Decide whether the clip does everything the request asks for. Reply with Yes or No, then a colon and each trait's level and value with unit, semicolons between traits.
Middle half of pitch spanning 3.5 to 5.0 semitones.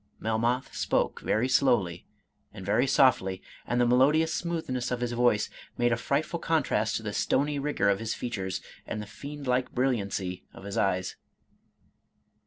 Yes: average, 4.3 semitones